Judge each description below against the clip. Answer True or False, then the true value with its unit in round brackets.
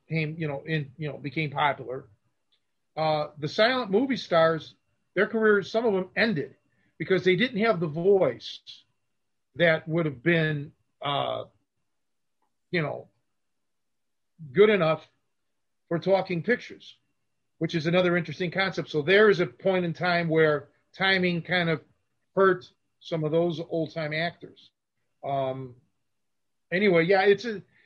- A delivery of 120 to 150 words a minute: True (140 wpm)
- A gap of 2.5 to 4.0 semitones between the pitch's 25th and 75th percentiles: True (3.7 semitones)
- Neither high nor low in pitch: True (170 Hz)